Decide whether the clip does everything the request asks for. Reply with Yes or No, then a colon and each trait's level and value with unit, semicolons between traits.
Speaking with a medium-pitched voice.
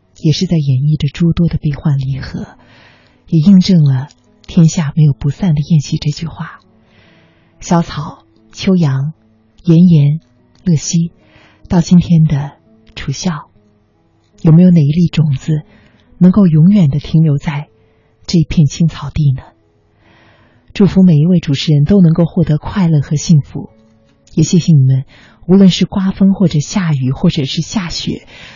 Yes: medium, 155 Hz